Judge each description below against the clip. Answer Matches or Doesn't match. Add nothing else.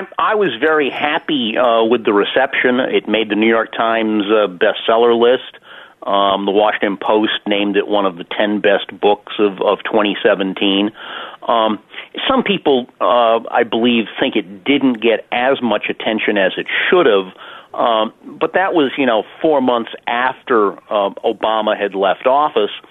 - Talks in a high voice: Doesn't match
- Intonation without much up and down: Matches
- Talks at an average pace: Matches